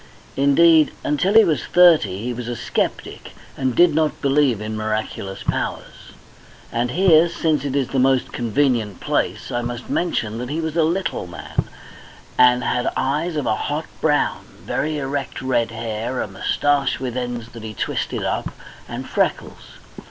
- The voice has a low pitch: Yes, low, 130 Hz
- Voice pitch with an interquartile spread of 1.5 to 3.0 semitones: No, average, 4.6 semitones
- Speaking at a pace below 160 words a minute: No, average, 165 wpm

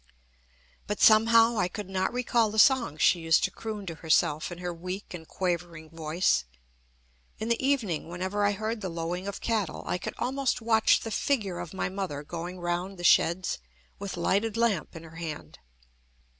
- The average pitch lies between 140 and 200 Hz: Yes, high, 190 Hz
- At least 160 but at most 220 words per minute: Yes, average, 180 wpm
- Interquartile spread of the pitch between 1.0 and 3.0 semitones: No, average, 4.4 semitones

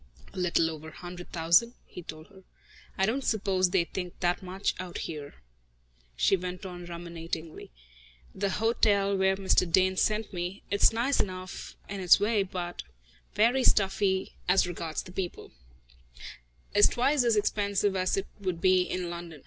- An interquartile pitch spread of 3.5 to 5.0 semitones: No, narrow, 2.5 semitones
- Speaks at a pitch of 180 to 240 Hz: Yes, medium, 185 Hz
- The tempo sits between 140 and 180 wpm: Yes, average, 160 wpm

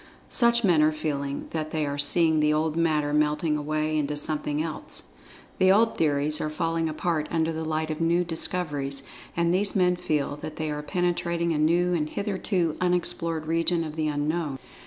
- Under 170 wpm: No, average, 175 wpm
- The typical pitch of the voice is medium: Yes, medium, 160 Hz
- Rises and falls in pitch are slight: Yes, narrow, 2.2 semitones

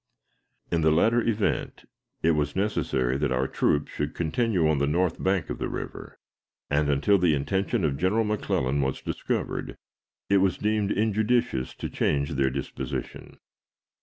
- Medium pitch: No, very low, 80 Hz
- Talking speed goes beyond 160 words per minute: No, average, 155 wpm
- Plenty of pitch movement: Yes, wide, 6.4 semitones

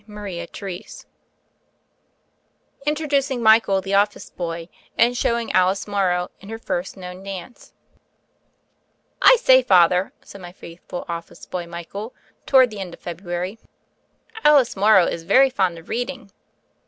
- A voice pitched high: Yes, high, 195 Hz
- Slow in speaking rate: Yes, slow, 130 wpm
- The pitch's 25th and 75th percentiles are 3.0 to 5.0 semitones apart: Yes, average, 4.7 semitones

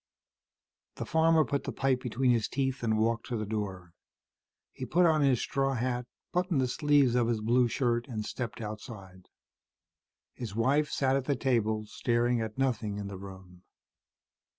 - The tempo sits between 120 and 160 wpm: No, average, 170 wpm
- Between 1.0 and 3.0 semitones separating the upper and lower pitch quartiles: No, average, 3.7 semitones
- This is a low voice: Yes, low, 120 Hz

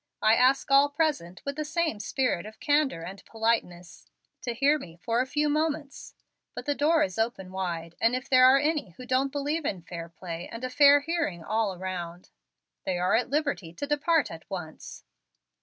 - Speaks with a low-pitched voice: No, very high, 250 Hz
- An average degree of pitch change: No, wide, 7.9 semitones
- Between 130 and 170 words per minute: No, average, 190 wpm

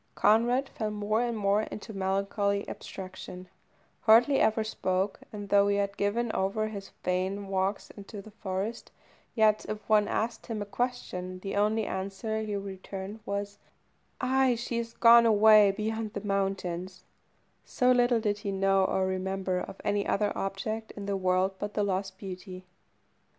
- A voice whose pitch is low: No, high, 205 Hz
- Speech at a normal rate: Yes, average, 160 wpm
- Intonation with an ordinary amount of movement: No, narrow, 2.2 semitones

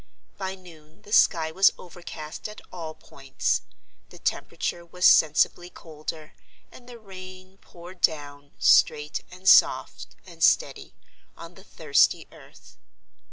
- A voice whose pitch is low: No, medium, 175 Hz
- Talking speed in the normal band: No, slow, 125 wpm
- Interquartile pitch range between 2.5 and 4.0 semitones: Yes, average, 3.3 semitones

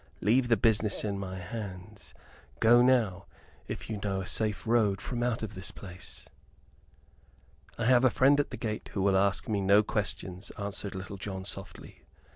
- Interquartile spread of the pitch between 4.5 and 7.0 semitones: No, average, 2.8 semitones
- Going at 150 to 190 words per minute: Yes, average, 175 wpm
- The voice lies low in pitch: Yes, low, 100 Hz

